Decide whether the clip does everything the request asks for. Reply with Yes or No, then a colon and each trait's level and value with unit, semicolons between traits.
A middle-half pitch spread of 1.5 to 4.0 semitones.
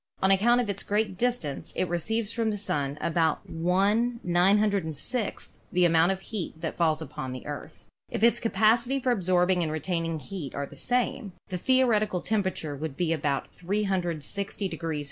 No: average, 4.9 semitones